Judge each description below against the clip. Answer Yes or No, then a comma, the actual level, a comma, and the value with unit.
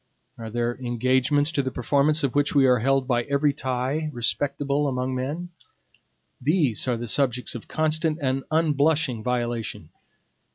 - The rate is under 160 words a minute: Yes, average, 150 wpm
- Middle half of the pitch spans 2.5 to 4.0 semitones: Yes, average, 2.9 semitones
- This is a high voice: No, low, 135 Hz